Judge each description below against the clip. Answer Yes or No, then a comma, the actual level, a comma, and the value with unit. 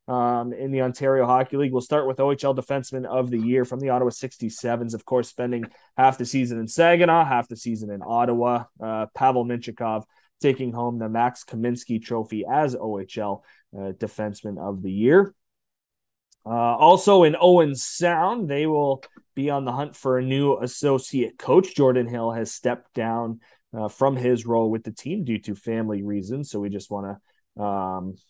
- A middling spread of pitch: Yes, average, 3.0 semitones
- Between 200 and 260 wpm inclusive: No, average, 180 wpm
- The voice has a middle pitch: No, low, 120 Hz